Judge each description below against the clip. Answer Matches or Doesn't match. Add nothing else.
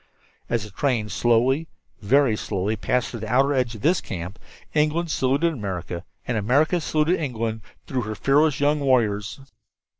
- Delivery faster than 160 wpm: Doesn't match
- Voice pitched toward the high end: Doesn't match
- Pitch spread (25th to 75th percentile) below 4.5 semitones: Doesn't match